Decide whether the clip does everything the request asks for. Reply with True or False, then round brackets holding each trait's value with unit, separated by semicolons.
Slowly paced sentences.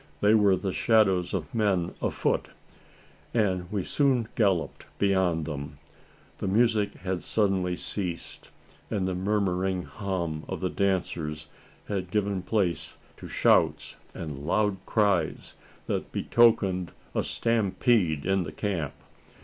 True (125 wpm)